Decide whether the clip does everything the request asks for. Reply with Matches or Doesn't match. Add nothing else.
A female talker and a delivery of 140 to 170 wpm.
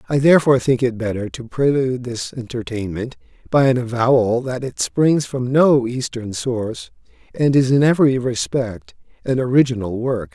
Doesn't match